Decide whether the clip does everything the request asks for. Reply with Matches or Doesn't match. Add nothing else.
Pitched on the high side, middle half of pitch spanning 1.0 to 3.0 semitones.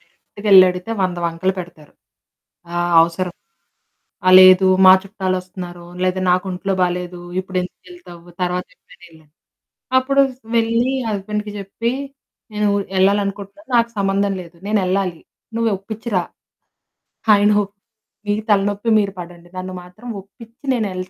Matches